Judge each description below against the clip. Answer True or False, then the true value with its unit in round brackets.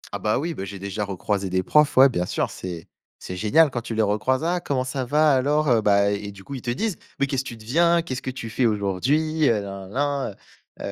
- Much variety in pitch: True (6.1 semitones)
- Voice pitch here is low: True (120 Hz)